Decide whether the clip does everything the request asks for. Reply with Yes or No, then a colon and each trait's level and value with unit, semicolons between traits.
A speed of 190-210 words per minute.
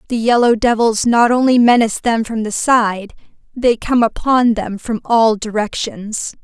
No: average, 160 wpm